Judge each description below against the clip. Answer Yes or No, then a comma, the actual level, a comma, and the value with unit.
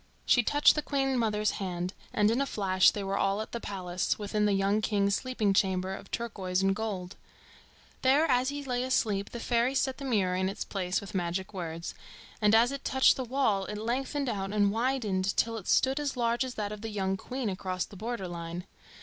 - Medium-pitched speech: No, high, 210 Hz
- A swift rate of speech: Yes, fast, 215 wpm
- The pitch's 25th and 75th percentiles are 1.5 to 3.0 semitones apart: No, average, 4.4 semitones